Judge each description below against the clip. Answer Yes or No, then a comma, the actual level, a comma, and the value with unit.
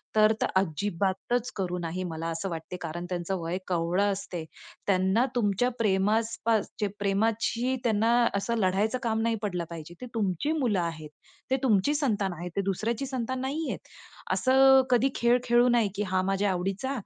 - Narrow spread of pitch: No, average, 4.3 semitones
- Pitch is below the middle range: No, high, 205 Hz